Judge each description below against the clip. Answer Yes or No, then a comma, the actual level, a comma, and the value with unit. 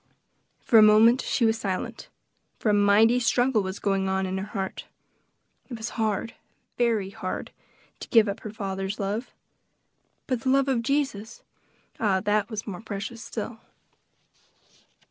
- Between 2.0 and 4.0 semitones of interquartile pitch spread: Yes, average, 2.8 semitones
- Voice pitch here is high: Yes, high, 215 Hz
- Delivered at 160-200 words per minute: No, average, 150 wpm